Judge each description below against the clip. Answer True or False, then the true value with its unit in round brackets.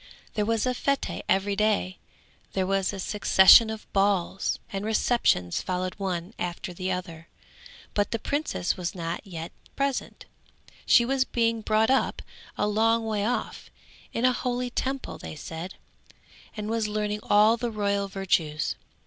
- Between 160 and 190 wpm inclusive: False (150 wpm)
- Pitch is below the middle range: False (205 Hz)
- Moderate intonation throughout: True (3.6 semitones)